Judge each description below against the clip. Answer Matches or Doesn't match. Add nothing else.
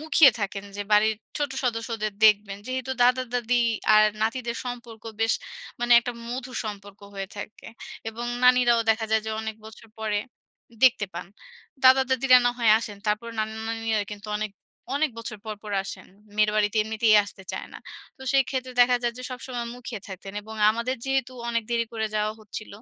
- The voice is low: Doesn't match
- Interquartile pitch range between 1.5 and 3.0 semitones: Matches